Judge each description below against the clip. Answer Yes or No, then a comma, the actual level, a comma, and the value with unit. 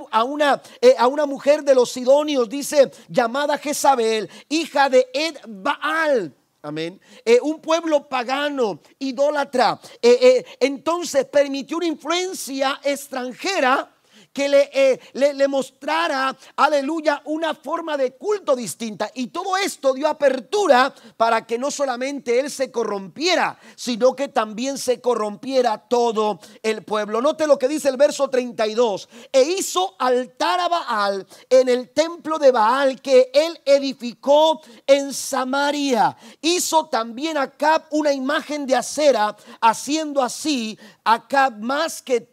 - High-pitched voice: Yes, very high, 275 Hz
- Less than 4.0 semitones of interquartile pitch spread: Yes, average, 3.4 semitones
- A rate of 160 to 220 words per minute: No, average, 140 wpm